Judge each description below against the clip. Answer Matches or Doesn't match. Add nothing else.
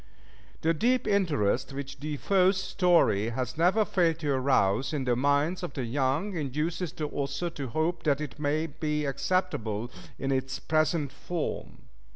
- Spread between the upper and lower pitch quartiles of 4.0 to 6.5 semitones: Matches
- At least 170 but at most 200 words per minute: Doesn't match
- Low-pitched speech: Doesn't match